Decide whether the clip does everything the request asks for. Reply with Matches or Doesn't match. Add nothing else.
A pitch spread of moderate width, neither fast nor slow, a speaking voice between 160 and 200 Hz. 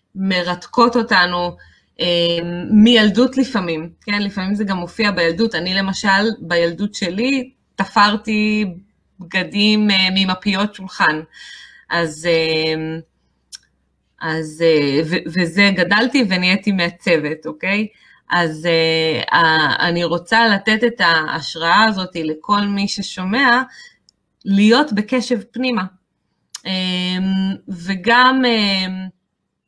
Doesn't match